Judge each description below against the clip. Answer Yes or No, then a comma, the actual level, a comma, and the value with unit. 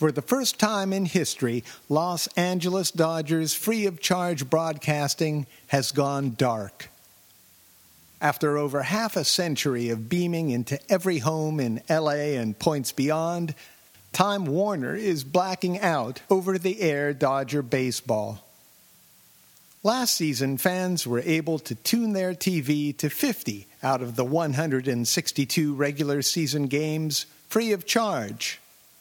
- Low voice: No, medium, 155 Hz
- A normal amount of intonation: Yes, average, 4.7 semitones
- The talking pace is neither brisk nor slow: No, slow, 130 wpm